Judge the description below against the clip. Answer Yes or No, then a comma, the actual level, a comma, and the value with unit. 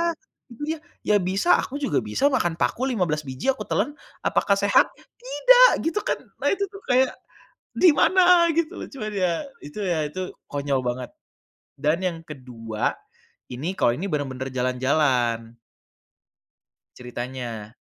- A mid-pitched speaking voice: Yes, medium, 165 Hz